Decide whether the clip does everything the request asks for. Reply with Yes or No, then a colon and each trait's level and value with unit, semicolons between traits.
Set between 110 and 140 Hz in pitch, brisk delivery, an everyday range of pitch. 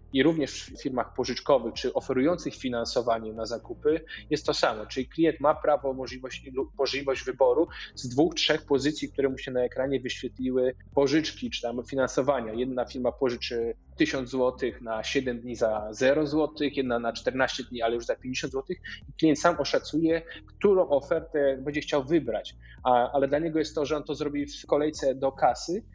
Yes: low, 135 Hz; fast, 175 wpm; average, 3.3 semitones